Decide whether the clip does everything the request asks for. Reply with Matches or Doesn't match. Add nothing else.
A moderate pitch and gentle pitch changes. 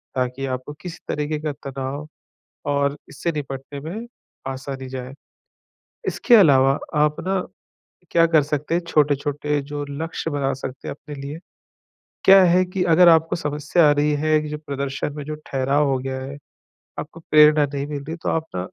Matches